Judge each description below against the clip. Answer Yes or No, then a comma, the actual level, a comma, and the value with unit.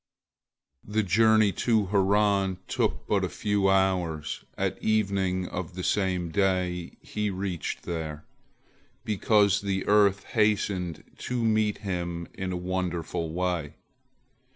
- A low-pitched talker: Yes, very low, 95 Hz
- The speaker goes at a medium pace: No, slow, 120 wpm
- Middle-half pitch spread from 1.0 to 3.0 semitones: Yes, narrow, 2.6 semitones